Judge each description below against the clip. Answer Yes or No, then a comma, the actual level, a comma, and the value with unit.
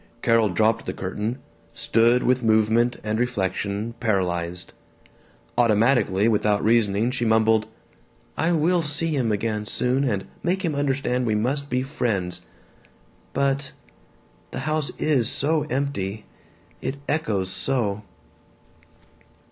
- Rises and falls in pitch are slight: No, average, 4.5 semitones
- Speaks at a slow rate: Yes, slow, 115 wpm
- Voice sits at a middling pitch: No, low, 115 Hz